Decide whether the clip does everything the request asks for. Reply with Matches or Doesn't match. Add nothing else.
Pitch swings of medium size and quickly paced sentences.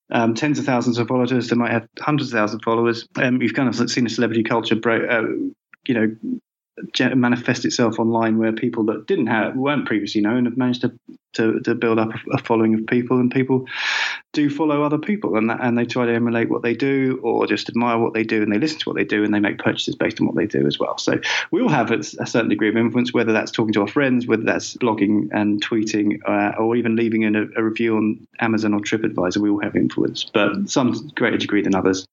Doesn't match